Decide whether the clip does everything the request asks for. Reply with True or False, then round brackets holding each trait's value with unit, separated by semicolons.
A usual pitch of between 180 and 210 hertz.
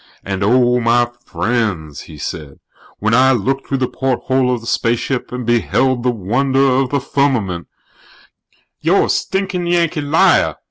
False (125 Hz)